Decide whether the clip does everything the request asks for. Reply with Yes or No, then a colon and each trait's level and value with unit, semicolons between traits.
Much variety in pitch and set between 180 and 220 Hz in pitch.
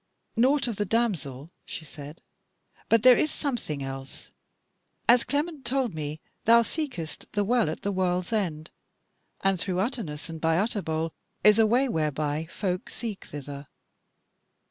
Yes: wide, 7.0 semitones; high, 190 Hz